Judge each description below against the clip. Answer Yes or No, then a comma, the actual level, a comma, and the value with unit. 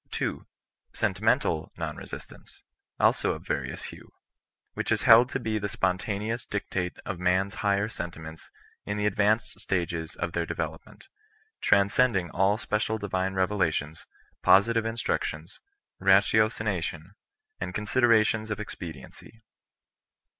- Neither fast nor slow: No, slow, 120 wpm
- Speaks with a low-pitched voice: Yes, low, 100 Hz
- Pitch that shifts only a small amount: No, average, 3.4 semitones